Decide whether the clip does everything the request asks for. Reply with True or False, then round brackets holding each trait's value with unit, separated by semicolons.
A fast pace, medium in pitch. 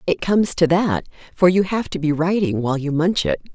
True (235 wpm; 170 Hz)